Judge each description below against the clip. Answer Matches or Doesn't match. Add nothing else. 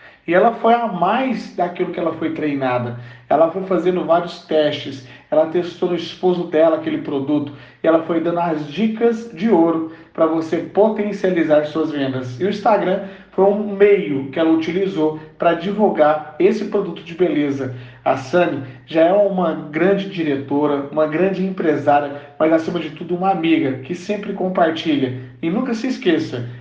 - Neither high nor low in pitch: Matches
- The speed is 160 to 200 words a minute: Matches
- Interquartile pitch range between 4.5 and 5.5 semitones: Doesn't match